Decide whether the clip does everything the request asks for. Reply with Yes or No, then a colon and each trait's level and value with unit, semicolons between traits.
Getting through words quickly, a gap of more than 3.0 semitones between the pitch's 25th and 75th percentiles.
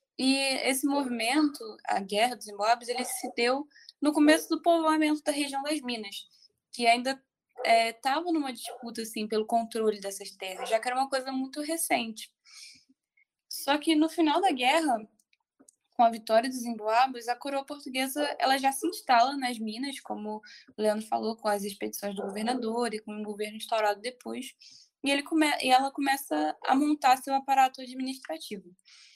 No: average, 165 wpm; average, 4.4 semitones